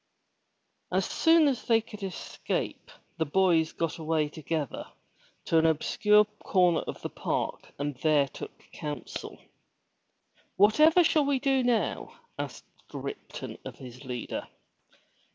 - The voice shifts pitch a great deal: Yes, wide, 7.2 semitones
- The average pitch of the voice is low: No, medium, 180 Hz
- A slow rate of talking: Yes, slow, 125 wpm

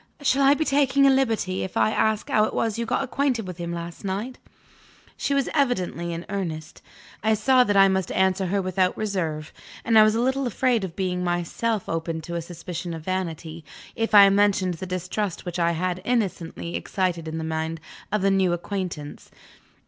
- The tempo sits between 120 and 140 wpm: No, average, 195 wpm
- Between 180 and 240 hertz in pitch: Yes, high, 190 Hz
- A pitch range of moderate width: Yes, average, 4.4 semitones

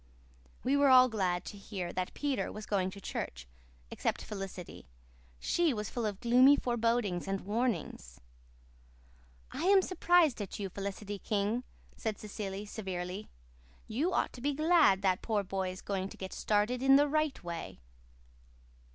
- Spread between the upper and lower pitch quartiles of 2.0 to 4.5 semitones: No, average, 5.0 semitones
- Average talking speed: Yes, average, 150 wpm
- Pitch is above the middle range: Yes, high, 210 Hz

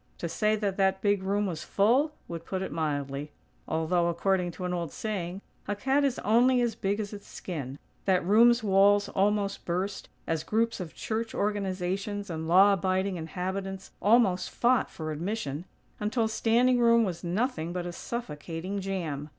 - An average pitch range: Yes, average, 3.7 semitones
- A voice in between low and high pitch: No, high, 195 Hz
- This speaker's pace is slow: No, average, 165 wpm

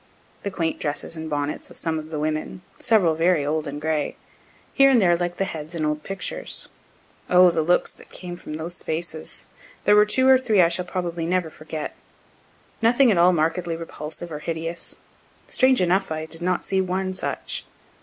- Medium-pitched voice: Yes, medium, 170 Hz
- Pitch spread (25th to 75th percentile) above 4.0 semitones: No, average, 2.8 semitones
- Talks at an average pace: Yes, average, 190 wpm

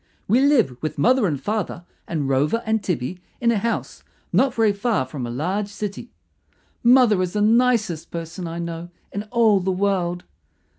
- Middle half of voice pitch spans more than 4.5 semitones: Yes, average, 5.2 semitones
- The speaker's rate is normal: Yes, average, 170 wpm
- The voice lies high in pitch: Yes, high, 200 Hz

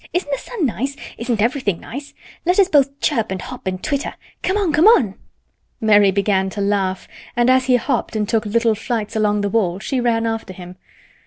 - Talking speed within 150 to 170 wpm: No, average, 200 wpm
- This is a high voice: Yes, high, 230 Hz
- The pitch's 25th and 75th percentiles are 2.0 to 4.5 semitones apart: No, average, 5.1 semitones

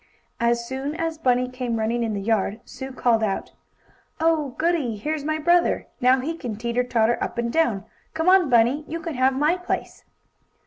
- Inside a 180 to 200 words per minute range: Yes, average, 185 wpm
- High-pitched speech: Yes, very high, 255 Hz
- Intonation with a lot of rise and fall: No, average, 5.0 semitones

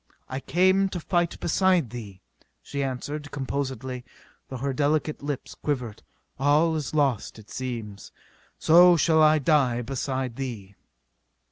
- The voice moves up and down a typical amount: Yes, average, 3.7 semitones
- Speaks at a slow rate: Yes, slow, 130 wpm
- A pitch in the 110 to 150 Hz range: Yes, medium, 140 Hz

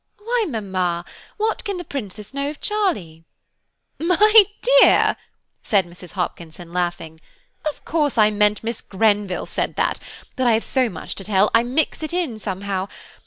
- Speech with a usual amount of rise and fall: No, wide, 8.9 semitones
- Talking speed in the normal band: Yes, average, 160 wpm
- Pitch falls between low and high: No, high, 215 Hz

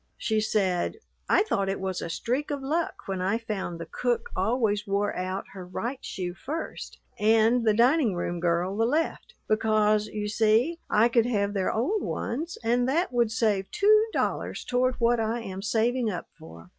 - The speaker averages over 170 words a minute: Yes, average, 180 wpm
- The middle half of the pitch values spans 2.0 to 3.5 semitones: No, average, 4.1 semitones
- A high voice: Yes, high, 220 Hz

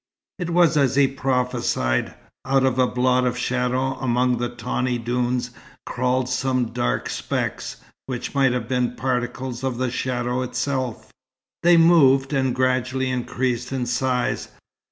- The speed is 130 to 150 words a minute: Yes, average, 140 wpm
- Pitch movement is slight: Yes, narrow, 1.2 semitones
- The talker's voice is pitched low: Yes, low, 125 Hz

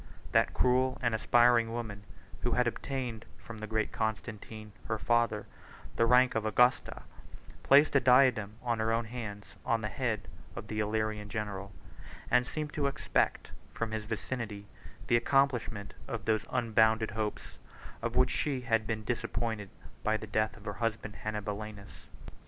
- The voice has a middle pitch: No, low, 110 Hz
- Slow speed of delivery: No, average, 155 wpm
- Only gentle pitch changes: Yes, narrow, 2.3 semitones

